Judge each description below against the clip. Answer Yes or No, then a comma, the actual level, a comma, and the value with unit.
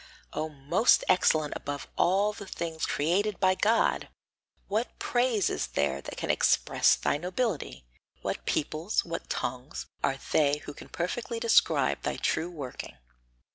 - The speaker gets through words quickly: No, average, 140 wpm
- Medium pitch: Yes, medium, 170 Hz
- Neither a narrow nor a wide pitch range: No, wide, 6.1 semitones